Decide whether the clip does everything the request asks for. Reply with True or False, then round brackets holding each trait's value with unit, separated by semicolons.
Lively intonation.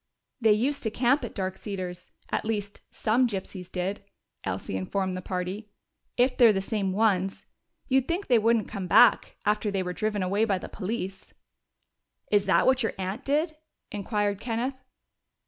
False (3.7 semitones)